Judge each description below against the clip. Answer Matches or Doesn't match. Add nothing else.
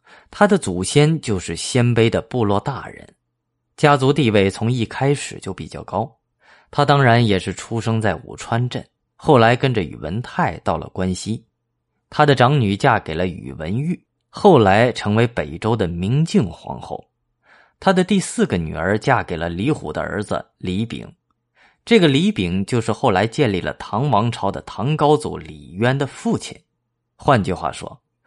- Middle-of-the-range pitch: Doesn't match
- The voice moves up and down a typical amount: Doesn't match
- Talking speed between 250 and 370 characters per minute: Doesn't match